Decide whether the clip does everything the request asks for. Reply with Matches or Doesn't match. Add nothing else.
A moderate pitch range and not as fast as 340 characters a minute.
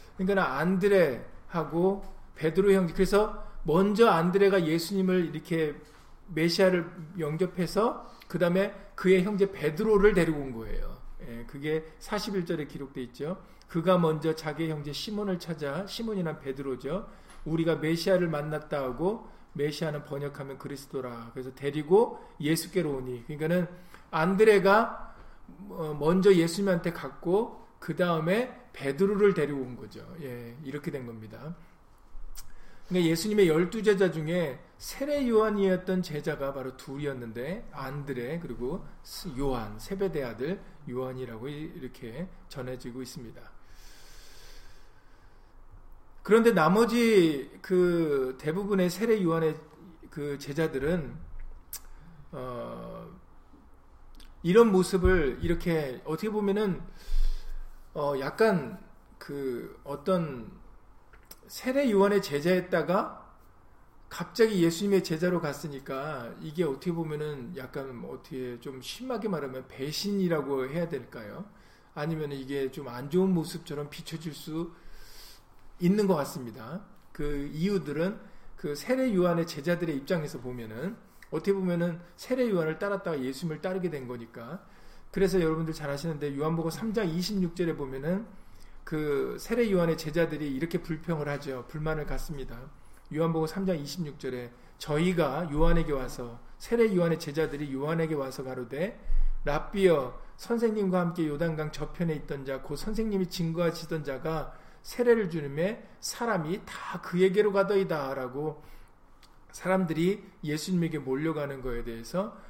Matches